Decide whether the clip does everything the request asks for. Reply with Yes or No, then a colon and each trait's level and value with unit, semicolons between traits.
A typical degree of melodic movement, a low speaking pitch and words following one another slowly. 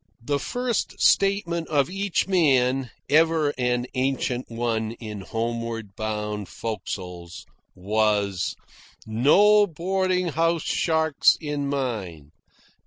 No: wide, 7.2 semitones; low, 130 Hz; slow, 100 wpm